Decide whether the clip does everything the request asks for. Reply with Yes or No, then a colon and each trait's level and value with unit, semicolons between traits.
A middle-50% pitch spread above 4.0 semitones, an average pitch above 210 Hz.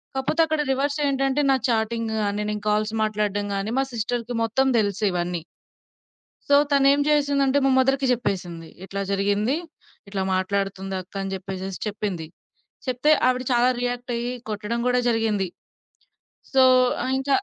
Yes: average, 4.9 semitones; high, 225 Hz